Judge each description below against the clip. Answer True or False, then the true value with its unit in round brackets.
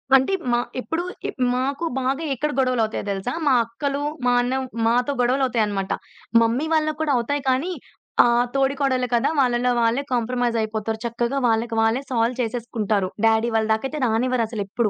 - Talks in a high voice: True (245 Hz)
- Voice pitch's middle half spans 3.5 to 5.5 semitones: False (2.9 semitones)